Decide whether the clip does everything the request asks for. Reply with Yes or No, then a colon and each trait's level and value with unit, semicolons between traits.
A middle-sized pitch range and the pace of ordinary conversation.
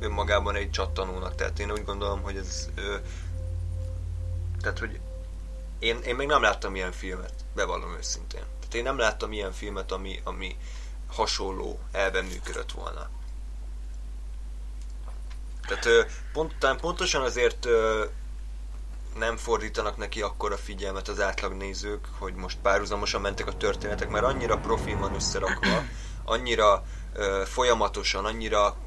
No: wide, 8.7 semitones; average, 130 wpm